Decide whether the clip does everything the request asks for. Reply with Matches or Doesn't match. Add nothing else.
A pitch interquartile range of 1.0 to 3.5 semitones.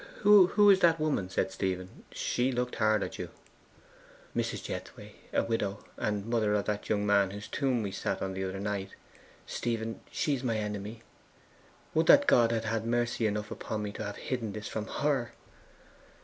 Matches